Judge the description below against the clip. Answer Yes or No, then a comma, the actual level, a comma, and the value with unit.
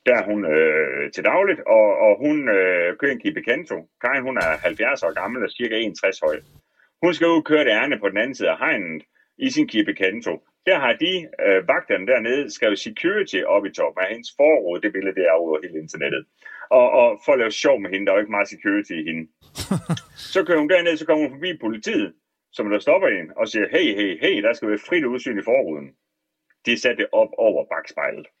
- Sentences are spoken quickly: Yes, fast, 230 wpm